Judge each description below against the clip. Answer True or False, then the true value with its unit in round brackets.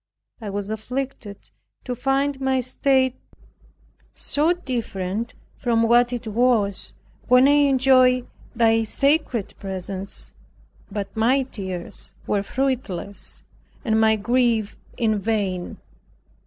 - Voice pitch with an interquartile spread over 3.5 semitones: True (4.1 semitones)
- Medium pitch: False (235 Hz)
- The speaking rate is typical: False (105 wpm)